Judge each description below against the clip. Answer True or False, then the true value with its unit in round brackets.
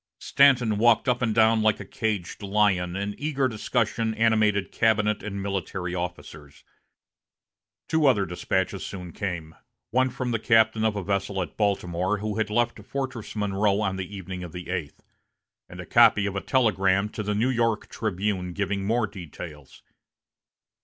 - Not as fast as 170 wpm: True (160 wpm)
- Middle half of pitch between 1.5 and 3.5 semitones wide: True (2.9 semitones)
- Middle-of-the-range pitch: False (105 Hz)